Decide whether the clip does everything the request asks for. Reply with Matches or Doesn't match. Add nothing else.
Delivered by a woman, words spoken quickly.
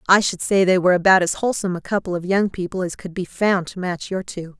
Matches